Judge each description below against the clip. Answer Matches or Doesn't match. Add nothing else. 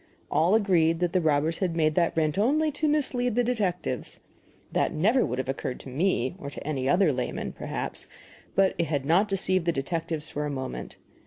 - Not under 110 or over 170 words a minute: Doesn't match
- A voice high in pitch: Doesn't match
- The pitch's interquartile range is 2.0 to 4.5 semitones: Doesn't match